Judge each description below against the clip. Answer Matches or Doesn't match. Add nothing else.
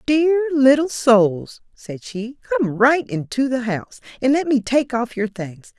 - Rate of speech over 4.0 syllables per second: Doesn't match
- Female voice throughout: Matches